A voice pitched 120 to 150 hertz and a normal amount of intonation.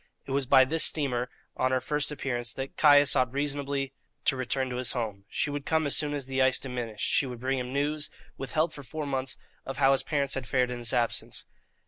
No: low, 135 Hz; narrow, 2.3 semitones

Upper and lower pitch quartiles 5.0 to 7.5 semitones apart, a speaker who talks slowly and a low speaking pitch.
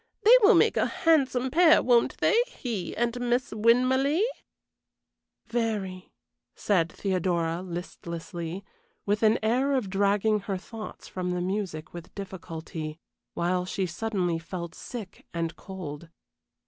No: average, 5.3 semitones; slow, 125 wpm; high, 195 Hz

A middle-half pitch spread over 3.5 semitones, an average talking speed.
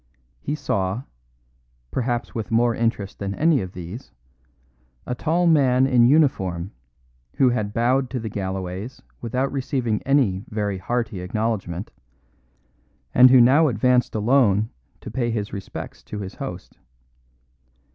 No: average, 4.4 semitones; slow, 130 wpm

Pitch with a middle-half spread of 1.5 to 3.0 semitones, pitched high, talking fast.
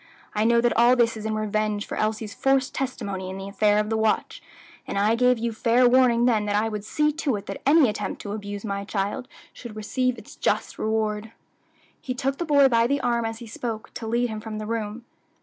Yes: narrow, 2.5 semitones; high, 225 Hz; fast, 230 wpm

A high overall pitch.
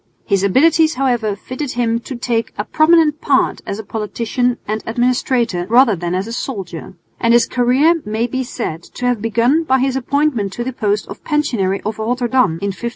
Yes: high, 240 Hz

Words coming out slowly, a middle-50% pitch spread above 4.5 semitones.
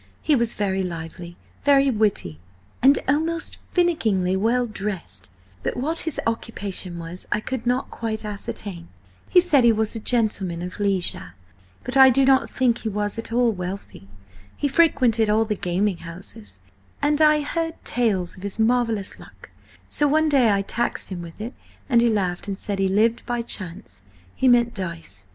No: average, 170 wpm; average, 5.0 semitones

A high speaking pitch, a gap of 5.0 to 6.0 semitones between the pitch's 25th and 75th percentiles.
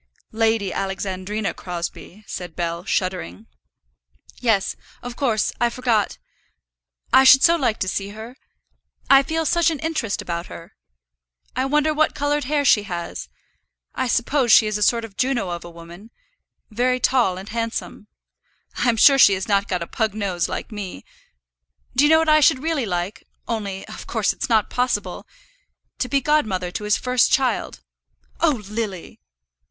Yes: high, 225 Hz; wide, 5.5 semitones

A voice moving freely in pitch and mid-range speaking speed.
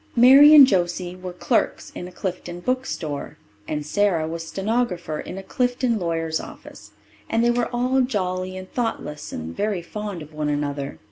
Yes: wide, 6.6 semitones; average, 165 wpm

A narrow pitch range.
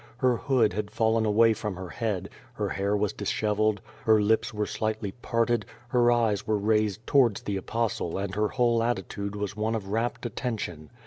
Yes: narrow, 2.1 semitones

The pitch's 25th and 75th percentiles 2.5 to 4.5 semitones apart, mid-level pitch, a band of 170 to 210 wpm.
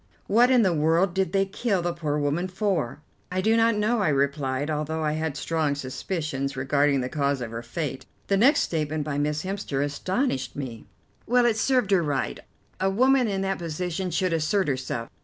No: wide, 5.4 semitones; medium, 160 Hz; average, 195 wpm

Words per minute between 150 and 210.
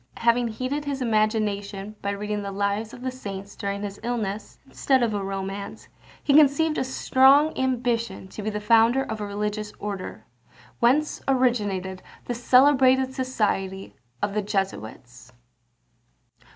No: average, 140 wpm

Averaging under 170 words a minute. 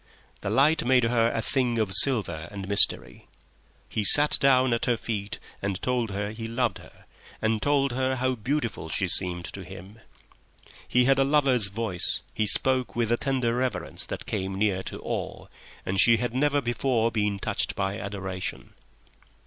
No: average, 175 wpm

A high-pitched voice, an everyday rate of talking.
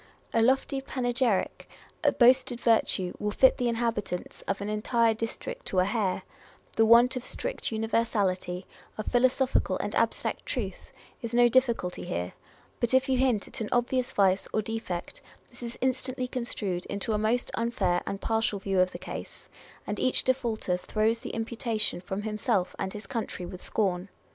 Yes: high, 225 Hz; average, 170 wpm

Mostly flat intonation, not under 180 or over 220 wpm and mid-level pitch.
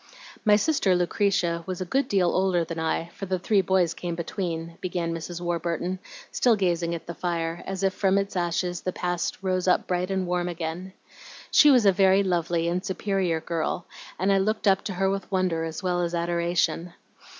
Yes: narrow, 2.0 semitones; average, 195 wpm; medium, 180 Hz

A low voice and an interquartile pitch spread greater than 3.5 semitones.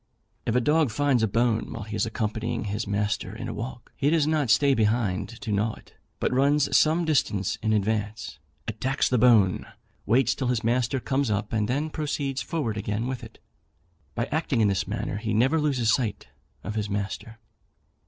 Yes: low, 115 Hz; average, 4.2 semitones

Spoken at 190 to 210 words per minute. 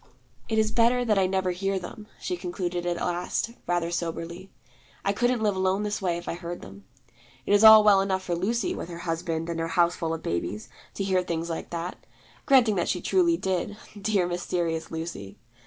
Yes: average, 200 wpm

